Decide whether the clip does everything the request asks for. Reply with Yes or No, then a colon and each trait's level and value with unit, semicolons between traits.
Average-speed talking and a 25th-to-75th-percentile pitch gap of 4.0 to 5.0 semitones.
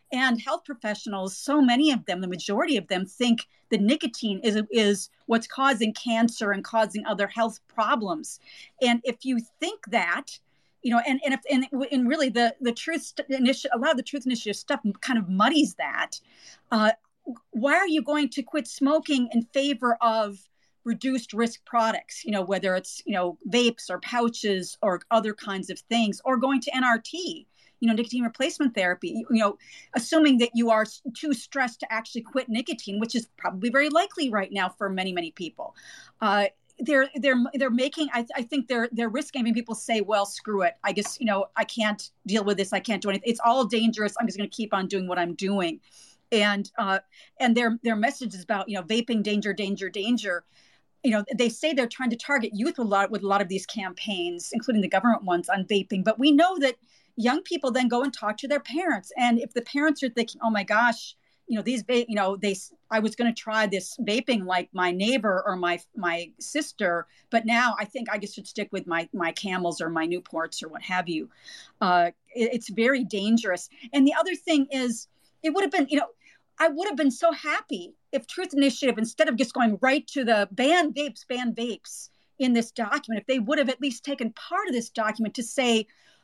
No: fast, 215 wpm; average, 4.6 semitones